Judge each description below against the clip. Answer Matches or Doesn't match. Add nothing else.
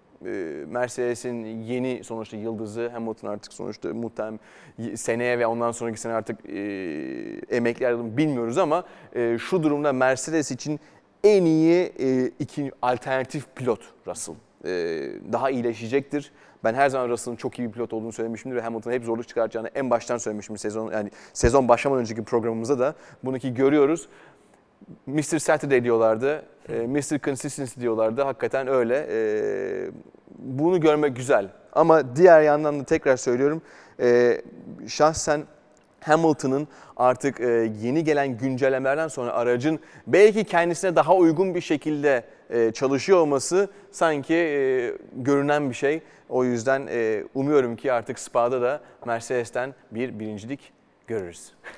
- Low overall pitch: Matches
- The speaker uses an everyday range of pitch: Matches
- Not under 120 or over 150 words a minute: Matches